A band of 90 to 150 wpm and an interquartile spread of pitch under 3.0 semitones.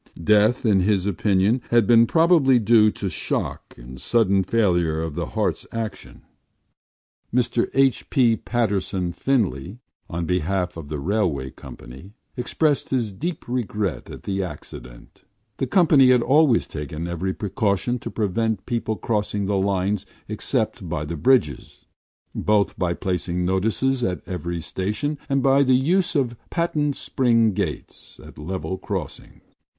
No: average, 140 wpm; average, 5.3 semitones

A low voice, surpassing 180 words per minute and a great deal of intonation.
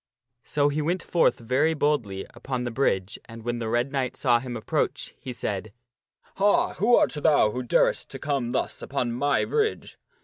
No: low, 125 Hz; average, 190 wpm; average, 3.8 semitones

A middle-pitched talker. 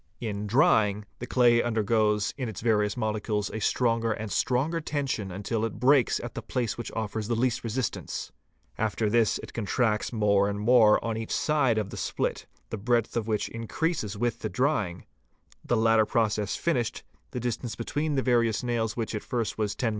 No: low, 115 Hz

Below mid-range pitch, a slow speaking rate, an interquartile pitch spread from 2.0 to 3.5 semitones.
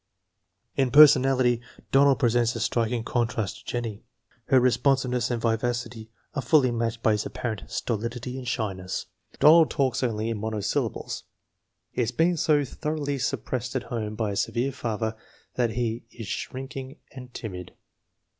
No: low, 120 Hz; average, 150 wpm; average, 2.8 semitones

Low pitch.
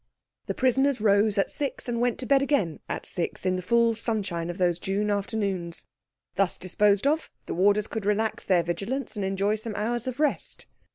No: high, 210 Hz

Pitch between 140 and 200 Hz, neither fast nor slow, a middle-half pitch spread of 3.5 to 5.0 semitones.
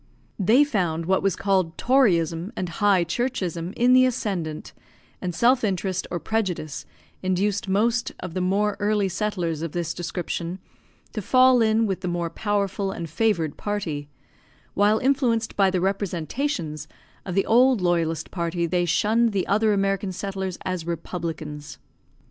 Yes: high, 190 Hz; average, 150 wpm; average, 3.9 semitones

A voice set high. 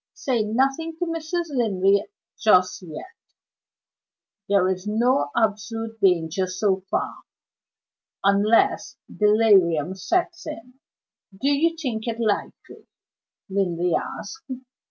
Yes: high, 215 Hz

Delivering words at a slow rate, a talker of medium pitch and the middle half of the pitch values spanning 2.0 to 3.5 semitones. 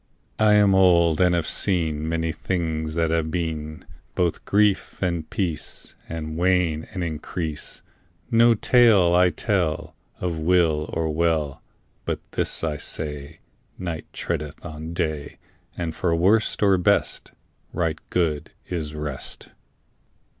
No: slow, 130 wpm; very low, 85 Hz; narrow, 2.5 semitones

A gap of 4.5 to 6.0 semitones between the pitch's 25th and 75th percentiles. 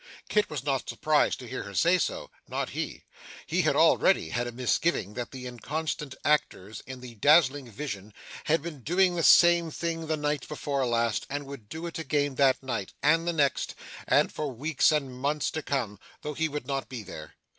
No: average, 4.0 semitones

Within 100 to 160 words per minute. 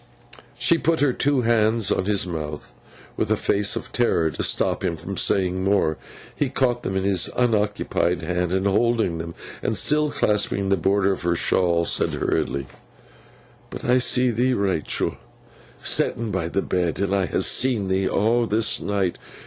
No: average, 170 wpm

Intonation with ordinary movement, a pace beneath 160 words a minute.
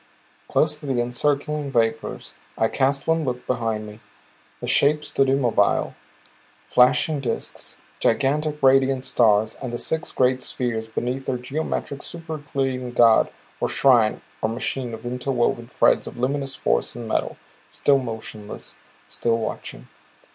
Yes: average, 3.0 semitones; average, 140 wpm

